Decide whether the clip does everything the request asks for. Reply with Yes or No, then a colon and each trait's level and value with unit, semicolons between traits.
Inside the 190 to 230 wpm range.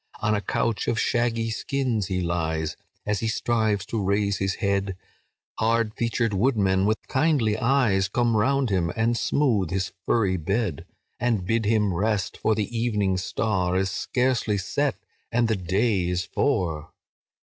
No: average, 155 wpm